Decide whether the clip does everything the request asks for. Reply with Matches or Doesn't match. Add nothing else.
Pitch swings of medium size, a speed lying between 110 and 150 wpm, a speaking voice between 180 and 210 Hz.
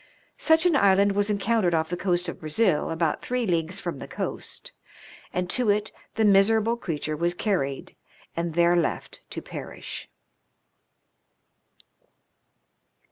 Matches